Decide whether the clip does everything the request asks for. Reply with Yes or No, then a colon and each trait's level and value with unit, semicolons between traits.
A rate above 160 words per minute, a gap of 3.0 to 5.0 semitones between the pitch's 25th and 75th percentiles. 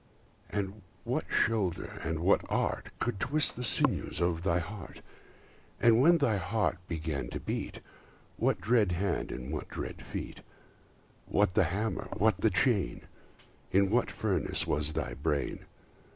No: average, 145 wpm; average, 4.7 semitones